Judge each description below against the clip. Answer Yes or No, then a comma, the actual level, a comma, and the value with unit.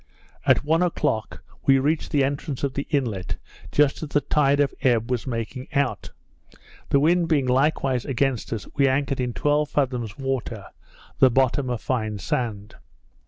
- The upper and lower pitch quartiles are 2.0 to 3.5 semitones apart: Yes, average, 2.8 semitones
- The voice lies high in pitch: No, low, 135 Hz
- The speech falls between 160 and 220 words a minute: Yes, average, 165 wpm